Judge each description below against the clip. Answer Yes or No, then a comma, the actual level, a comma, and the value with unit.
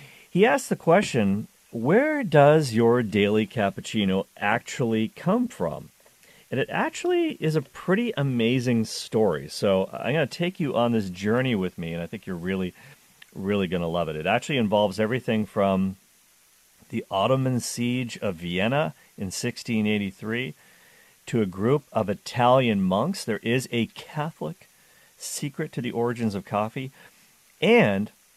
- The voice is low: Yes, low, 115 Hz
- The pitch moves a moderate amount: No, wide, 6.3 semitones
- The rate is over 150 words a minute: No, average, 145 wpm